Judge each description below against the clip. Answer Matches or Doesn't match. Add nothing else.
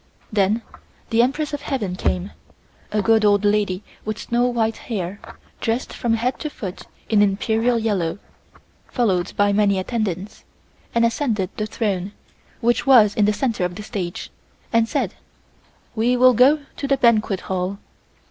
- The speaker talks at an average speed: Matches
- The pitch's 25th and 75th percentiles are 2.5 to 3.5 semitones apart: Matches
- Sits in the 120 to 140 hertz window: Doesn't match